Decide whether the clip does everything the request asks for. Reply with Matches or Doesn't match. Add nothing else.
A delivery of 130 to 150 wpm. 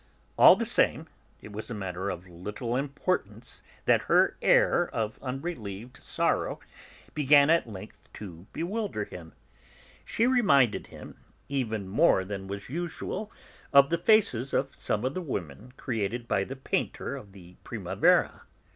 Matches